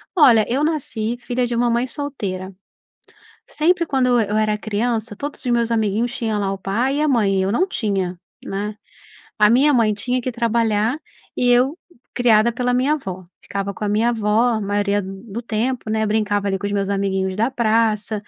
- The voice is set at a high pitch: Yes, high, 225 Hz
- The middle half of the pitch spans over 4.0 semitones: No, average, 3.2 semitones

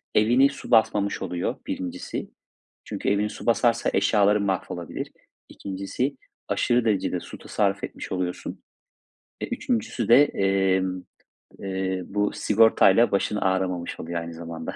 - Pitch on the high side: No, low, 100 Hz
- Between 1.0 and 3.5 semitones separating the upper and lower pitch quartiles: Yes, average, 2.7 semitones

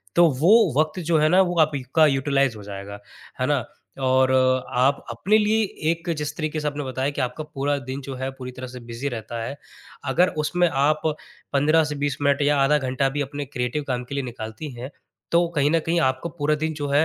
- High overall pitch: No, medium, 145 Hz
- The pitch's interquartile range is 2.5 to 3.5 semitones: Yes, average, 3.1 semitones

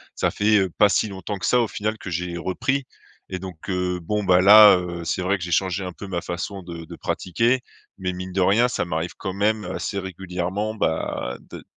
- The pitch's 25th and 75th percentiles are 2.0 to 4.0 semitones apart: Yes, average, 2.7 semitones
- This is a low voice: Yes, very low, 95 Hz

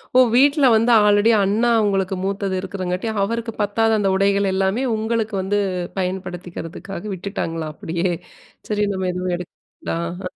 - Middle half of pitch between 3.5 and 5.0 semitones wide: No, average, 2.7 semitones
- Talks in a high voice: Yes, high, 195 Hz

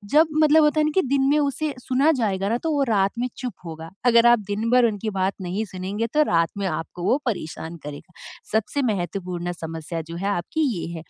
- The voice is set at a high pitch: Yes, high, 205 Hz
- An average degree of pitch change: No, wide, 7.2 semitones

